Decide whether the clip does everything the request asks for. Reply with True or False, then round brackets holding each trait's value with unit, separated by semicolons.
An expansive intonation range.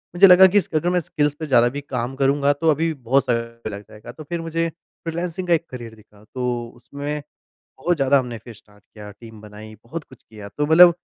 True (5.9 semitones)